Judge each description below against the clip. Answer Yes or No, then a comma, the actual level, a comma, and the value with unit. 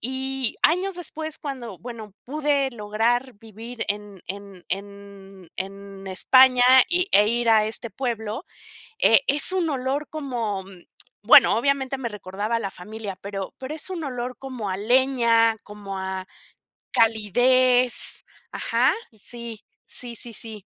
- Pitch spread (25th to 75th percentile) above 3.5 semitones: Yes, average, 4.4 semitones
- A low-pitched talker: No, high, 230 Hz